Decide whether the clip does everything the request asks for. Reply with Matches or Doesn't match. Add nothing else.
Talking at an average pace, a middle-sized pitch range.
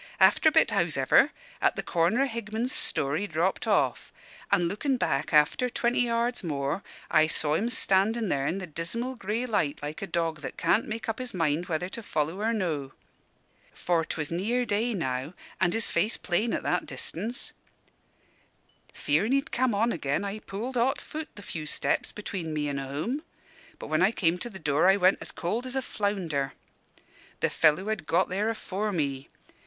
Doesn't match